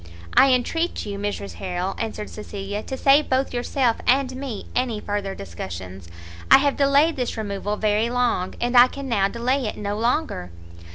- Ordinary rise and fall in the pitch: Yes, average, 4.7 semitones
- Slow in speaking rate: No, average, 170 wpm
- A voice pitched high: Yes, high, 230 Hz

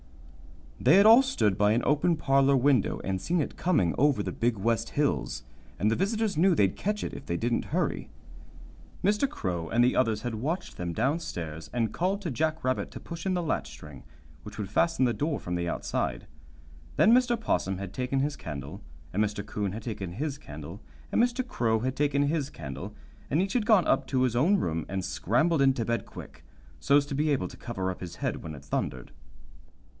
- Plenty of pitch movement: Yes, wide, 8.8 semitones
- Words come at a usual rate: No, fast, 210 wpm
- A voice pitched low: Yes, low, 125 Hz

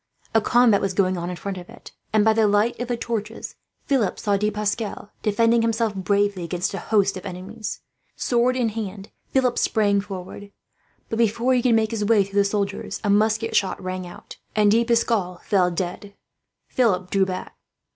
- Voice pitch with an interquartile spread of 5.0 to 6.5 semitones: No, narrow, 2.6 semitones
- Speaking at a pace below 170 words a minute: No, average, 190 wpm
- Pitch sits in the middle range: No, high, 205 Hz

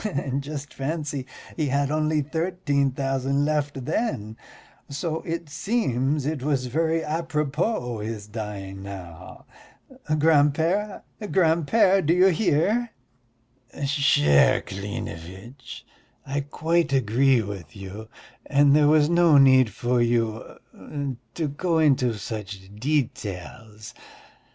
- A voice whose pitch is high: No, medium, 140 Hz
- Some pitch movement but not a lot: No, wide, 5.7 semitones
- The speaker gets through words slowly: Yes, slow, 110 wpm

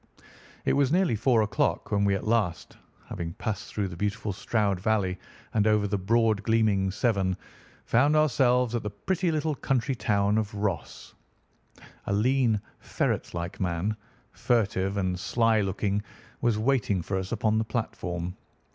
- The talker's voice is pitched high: No, low, 105 Hz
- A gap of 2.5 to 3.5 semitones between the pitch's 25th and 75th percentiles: Yes, average, 3.2 semitones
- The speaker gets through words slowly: No, average, 155 wpm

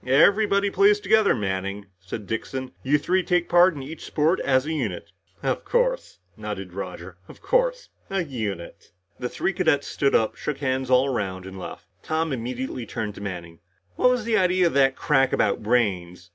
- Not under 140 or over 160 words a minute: No, average, 185 wpm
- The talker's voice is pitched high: No, low, 130 Hz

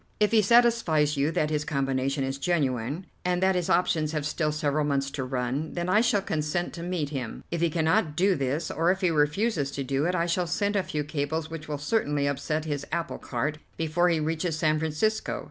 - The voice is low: No, medium, 155 Hz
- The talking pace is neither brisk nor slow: No, fast, 215 wpm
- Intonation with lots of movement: No, average, 3.3 semitones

